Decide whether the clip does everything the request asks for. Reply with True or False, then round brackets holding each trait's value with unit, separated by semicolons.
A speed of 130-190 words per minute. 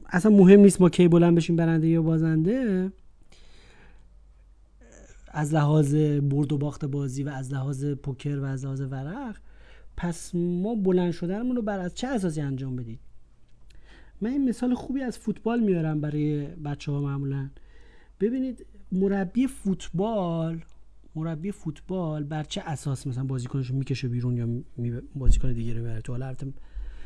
True (150 wpm)